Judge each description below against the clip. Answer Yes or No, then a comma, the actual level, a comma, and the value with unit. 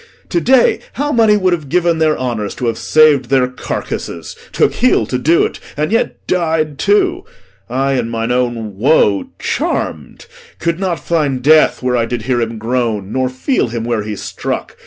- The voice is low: Yes, low, 130 Hz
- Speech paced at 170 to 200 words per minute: Yes, average, 180 wpm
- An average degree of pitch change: No, wide, 6.3 semitones